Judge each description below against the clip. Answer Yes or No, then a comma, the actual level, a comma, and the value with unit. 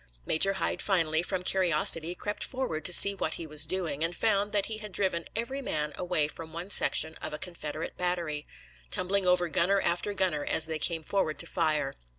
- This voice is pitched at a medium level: Yes, medium, 175 Hz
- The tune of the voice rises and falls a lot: No, average, 3.6 semitones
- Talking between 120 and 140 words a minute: No, average, 195 wpm